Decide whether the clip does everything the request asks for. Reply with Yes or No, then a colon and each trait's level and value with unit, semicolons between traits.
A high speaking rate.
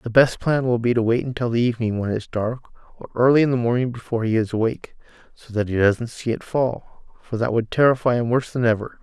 Yes: fast, 255 wpm